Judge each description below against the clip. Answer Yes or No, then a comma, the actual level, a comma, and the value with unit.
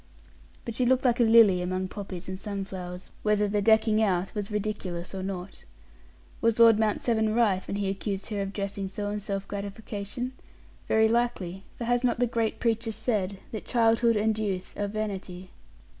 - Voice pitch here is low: No, high, 210 Hz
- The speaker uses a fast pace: No, average, 180 wpm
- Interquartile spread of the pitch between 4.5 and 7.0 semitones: No, narrow, 2.6 semitones